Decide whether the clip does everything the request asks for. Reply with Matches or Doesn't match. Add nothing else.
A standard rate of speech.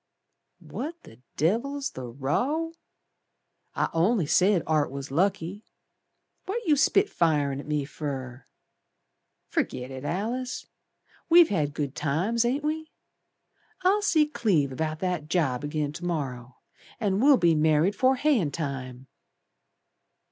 Doesn't match